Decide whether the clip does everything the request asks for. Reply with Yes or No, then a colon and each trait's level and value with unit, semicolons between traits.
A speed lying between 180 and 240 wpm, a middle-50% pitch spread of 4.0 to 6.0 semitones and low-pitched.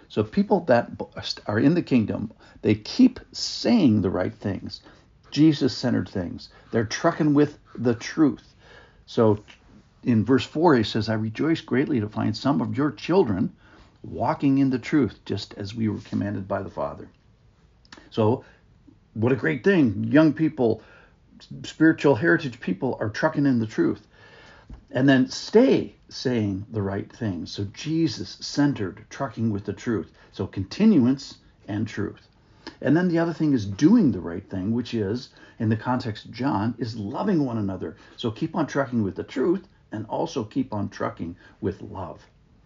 No: average, 165 wpm; average, 5.2 semitones; low, 115 Hz